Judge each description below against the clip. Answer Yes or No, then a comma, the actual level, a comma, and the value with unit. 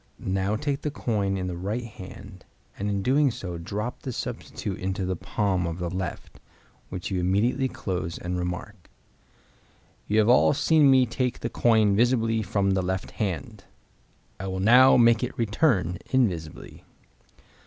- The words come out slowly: No, average, 160 wpm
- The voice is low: Yes, low, 100 Hz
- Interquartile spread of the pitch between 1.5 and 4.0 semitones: No, average, 4.5 semitones